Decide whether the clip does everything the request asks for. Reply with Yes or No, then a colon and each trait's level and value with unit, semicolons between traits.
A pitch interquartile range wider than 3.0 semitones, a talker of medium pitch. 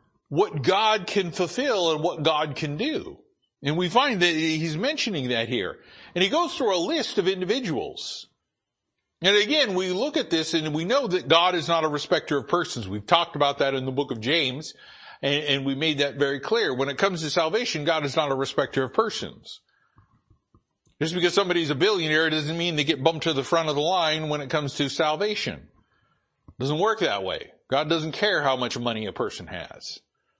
Yes: average, 3.8 semitones; medium, 160 Hz